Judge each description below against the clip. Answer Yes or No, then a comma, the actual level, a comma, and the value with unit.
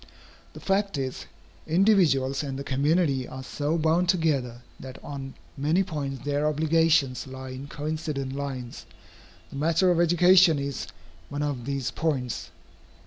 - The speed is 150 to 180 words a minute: No, average, 140 wpm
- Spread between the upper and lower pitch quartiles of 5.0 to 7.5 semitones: No, average, 3.5 semitones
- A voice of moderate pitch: Yes, medium, 145 Hz